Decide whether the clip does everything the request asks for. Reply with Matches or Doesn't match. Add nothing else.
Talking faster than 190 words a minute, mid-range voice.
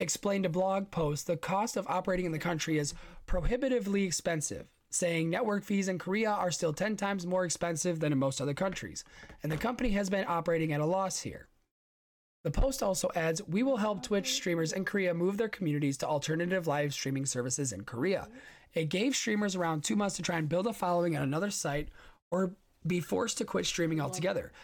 Matches